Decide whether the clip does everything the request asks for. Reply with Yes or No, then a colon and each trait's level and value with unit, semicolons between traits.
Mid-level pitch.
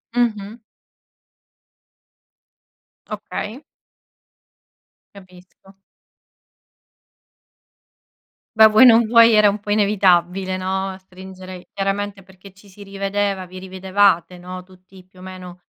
No: high, 195 Hz